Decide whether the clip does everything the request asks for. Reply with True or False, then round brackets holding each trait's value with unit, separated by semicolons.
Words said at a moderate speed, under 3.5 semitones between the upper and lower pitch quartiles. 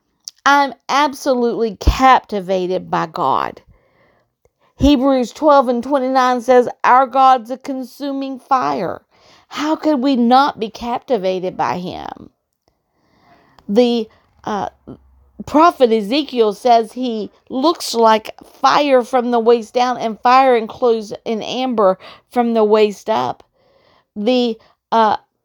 False (115 wpm; 3.0 semitones)